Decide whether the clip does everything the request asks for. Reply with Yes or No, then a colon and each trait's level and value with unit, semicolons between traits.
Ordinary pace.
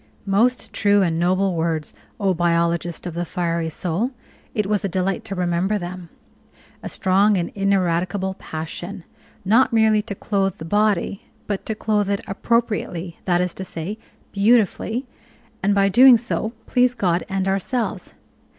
Yes: average, 150 wpm